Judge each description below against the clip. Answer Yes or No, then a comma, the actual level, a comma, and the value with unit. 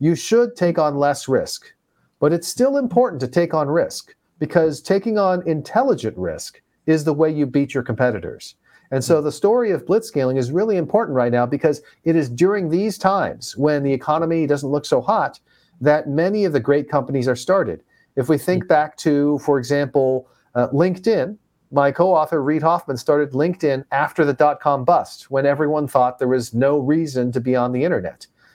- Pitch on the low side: No, medium, 150 Hz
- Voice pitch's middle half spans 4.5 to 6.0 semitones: No, average, 3.8 semitones